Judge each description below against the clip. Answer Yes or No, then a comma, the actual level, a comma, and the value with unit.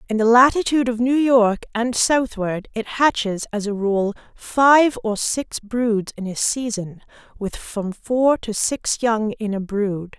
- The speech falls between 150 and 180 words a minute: Yes, average, 170 wpm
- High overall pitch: Yes, high, 230 Hz